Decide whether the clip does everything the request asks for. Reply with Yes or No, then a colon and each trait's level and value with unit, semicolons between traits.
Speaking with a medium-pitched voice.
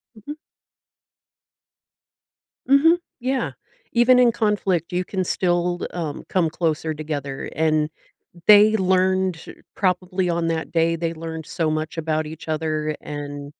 Yes: medium, 170 Hz